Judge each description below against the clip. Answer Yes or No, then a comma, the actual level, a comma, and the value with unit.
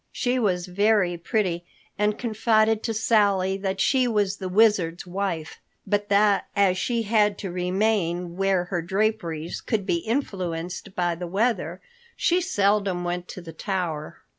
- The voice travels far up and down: No, average, 3.4 semitones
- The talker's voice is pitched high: Yes, high, 195 Hz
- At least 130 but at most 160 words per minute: Yes, average, 150 wpm